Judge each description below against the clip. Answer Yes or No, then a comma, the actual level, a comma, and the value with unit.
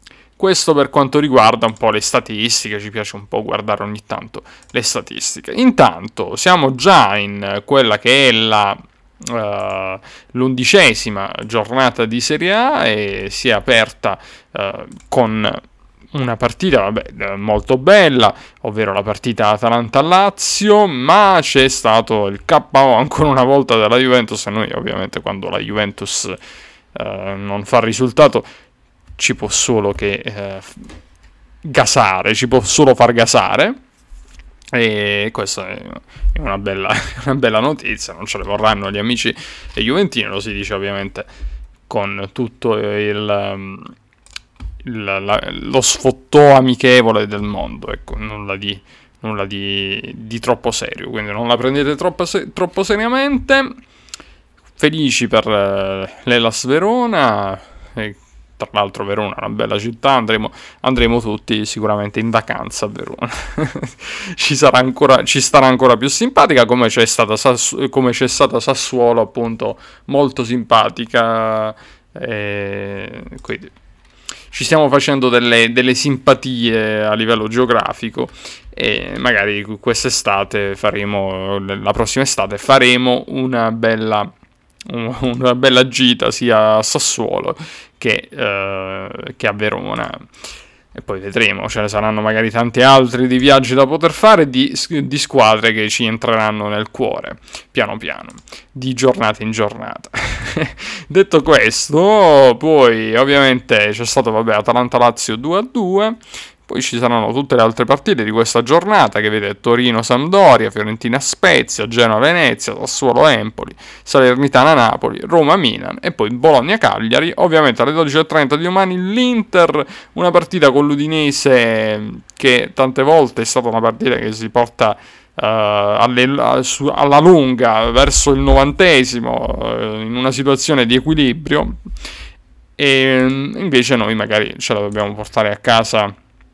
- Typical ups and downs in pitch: Yes, average, 4.3 semitones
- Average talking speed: Yes, average, 130 wpm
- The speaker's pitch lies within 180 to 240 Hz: No, low, 120 Hz